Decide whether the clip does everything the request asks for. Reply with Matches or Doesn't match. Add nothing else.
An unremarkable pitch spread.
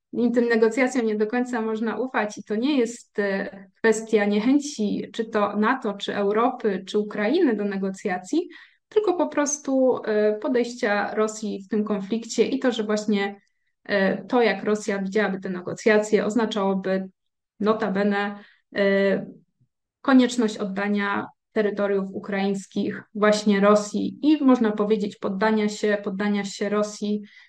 Doesn't match